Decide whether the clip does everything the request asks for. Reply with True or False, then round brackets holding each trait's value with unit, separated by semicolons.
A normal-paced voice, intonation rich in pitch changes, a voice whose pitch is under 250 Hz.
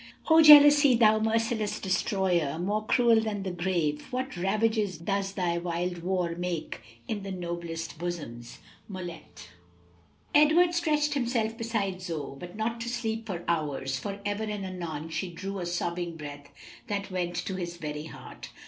False (155 wpm; 4.5 semitones; 190 Hz)